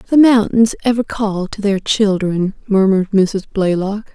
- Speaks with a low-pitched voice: No, high, 205 Hz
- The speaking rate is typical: Yes, average, 145 wpm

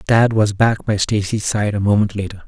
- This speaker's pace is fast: Yes, fast, 220 wpm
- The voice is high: No, low, 105 Hz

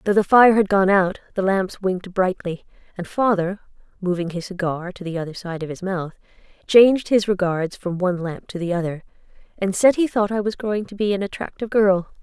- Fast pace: Yes, fast, 210 wpm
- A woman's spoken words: Yes, female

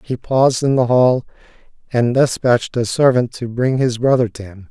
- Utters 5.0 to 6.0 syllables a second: Yes, 5.1 syllables/s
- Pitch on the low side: Yes, low, 125 Hz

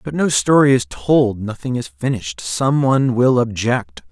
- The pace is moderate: Yes, average, 175 wpm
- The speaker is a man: Yes, male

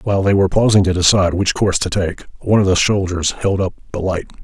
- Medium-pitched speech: No, very low, 95 Hz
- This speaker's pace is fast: Yes, fast, 245 wpm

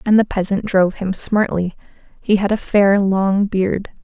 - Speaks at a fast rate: No, average, 180 wpm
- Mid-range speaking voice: No, high, 195 Hz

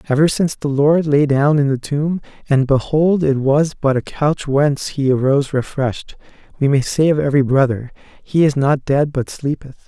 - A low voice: No, medium, 145 Hz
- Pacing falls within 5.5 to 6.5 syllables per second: No, 5.1 syllables/s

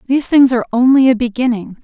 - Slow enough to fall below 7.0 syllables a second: No, 7.1 syllables/s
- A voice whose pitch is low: No, high, 245 Hz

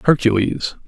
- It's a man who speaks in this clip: Yes, male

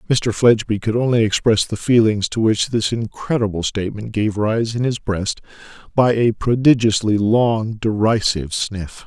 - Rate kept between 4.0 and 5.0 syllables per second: Yes, 4.7 syllables/s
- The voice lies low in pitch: Yes, low, 110 Hz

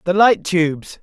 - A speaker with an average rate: Yes, average, 175 wpm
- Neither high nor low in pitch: Yes, medium, 180 Hz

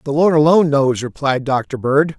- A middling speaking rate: Yes, average, 190 wpm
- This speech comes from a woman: No, male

